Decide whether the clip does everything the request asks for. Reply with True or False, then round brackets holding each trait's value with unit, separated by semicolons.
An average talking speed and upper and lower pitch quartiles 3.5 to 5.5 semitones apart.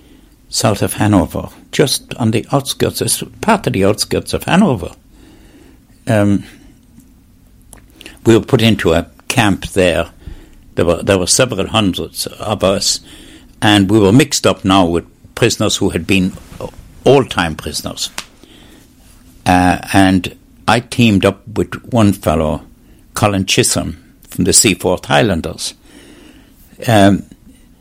False (125 wpm; 4.0 semitones)